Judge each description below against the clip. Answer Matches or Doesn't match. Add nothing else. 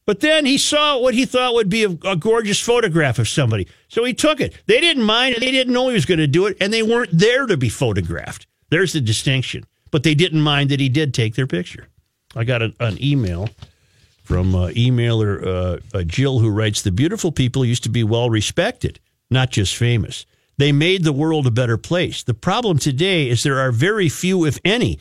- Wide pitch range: Matches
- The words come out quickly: Matches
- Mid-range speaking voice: Matches